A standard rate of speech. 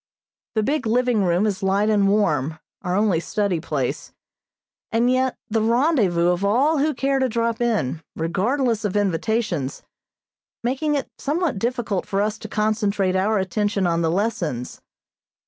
Yes: average, 150 wpm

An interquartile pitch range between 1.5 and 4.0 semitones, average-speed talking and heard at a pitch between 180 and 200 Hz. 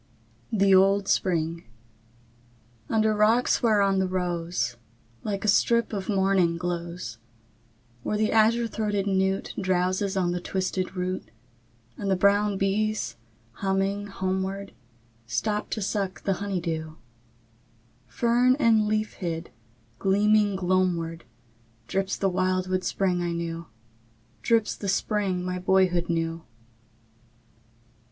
No: narrow, 2.5 semitones; slow, 115 wpm; high, 190 Hz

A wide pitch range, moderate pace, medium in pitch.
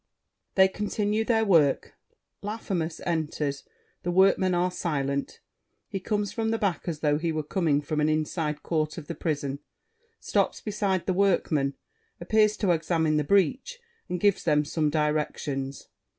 No: average, 4.6 semitones; average, 150 wpm; medium, 170 Hz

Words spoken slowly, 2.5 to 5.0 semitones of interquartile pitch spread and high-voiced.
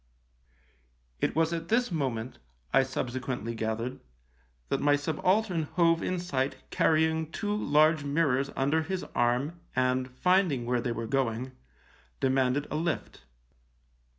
No: slow, 130 wpm; average, 4.6 semitones; medium, 140 Hz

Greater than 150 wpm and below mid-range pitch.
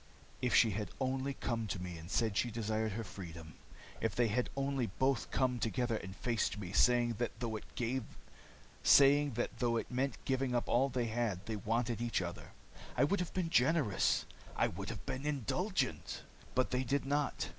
Yes: average, 175 wpm; low, 120 Hz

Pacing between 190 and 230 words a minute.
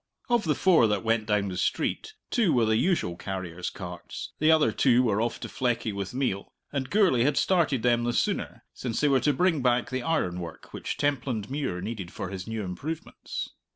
Yes: average, 195 wpm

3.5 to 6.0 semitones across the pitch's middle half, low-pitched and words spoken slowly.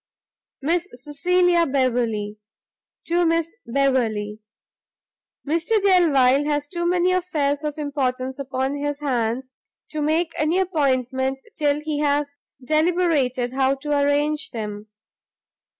No: average, 3.9 semitones; very high, 285 Hz; slow, 110 wpm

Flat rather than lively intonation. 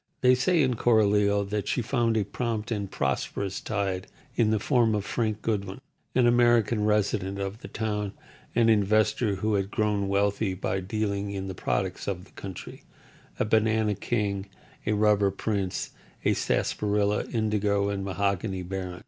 Yes: narrow, 1.9 semitones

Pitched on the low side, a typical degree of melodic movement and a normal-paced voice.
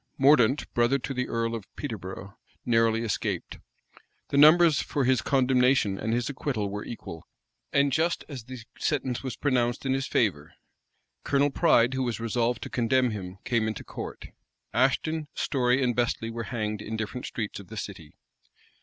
Yes: low, 120 Hz; average, 3.3 semitones; average, 165 wpm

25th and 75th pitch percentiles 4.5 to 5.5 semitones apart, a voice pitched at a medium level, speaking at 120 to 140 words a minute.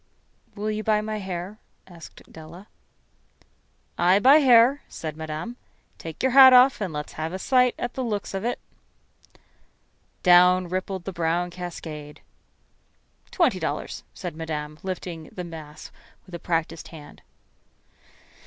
Yes: average, 4.9 semitones; medium, 180 Hz; slow, 135 wpm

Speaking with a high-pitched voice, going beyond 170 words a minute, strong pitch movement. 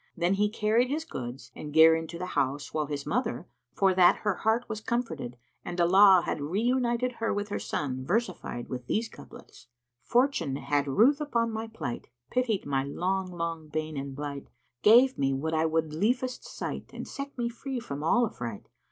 No: medium, 180 Hz; average, 190 wpm; wide, 8.0 semitones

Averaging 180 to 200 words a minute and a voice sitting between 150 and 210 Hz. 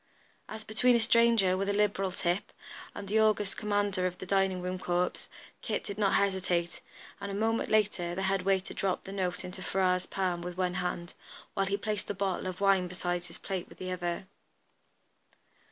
Yes: average, 190 wpm; high, 190 Hz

